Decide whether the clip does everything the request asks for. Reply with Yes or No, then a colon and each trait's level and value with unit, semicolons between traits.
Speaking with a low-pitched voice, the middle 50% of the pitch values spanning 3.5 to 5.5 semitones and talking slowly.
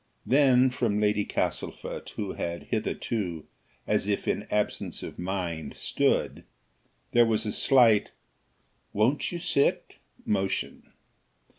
Yes: low, 105 Hz; average, 3.8 semitones; slow, 115 wpm